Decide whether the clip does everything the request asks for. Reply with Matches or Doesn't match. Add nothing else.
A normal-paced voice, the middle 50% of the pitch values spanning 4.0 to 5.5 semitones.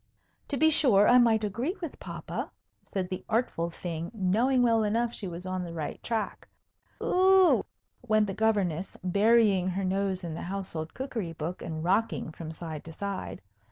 Matches